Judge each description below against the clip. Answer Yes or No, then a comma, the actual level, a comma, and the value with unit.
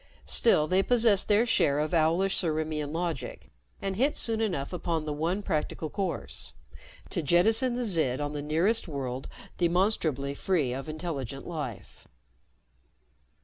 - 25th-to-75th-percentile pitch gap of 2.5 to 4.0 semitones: No, average, 4.9 semitones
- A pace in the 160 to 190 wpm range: No, average, 140 wpm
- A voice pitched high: No, medium, 165 Hz